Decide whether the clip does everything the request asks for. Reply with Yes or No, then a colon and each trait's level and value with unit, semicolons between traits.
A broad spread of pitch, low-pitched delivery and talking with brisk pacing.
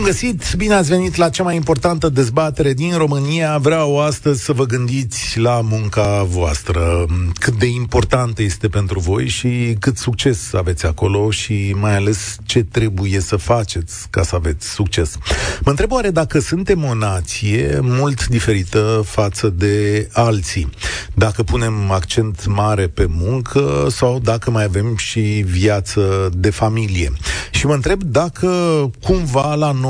No: wide, 5.8 semitones; low, 110 Hz; average, 150 wpm